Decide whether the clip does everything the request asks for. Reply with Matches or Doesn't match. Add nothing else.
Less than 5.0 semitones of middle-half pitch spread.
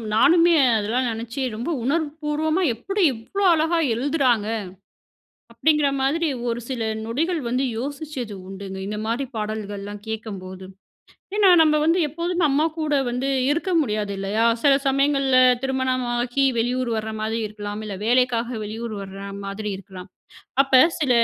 Doesn't match